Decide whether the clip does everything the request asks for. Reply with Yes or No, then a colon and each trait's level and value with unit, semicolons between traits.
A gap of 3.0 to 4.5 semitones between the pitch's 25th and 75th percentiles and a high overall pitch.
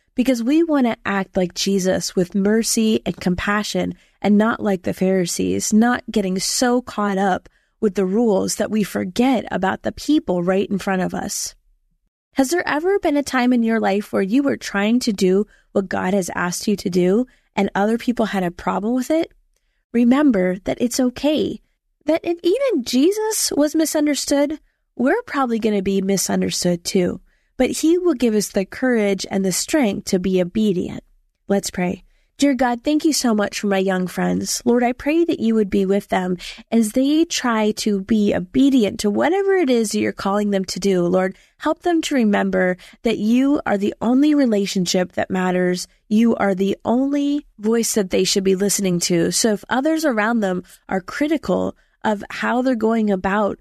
No: average, 5.2 semitones; high, 215 Hz